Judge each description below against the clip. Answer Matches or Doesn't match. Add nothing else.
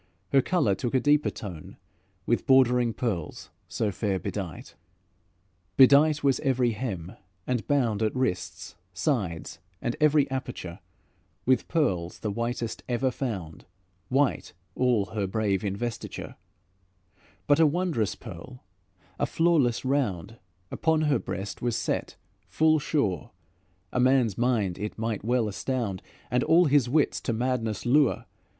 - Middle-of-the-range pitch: Doesn't match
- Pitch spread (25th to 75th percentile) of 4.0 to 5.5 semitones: Matches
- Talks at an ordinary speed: Doesn't match